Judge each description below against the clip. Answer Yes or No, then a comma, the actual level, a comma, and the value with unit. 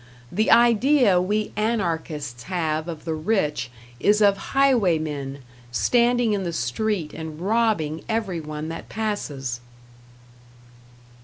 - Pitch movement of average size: No, wide, 6.1 semitones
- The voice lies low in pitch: No, medium, 180 Hz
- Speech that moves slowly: Yes, slow, 110 wpm